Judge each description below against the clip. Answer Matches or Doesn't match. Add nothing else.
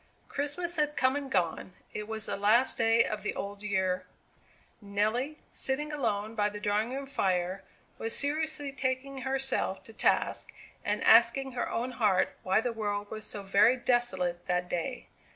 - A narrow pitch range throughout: Doesn't match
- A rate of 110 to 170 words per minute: Matches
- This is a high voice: Matches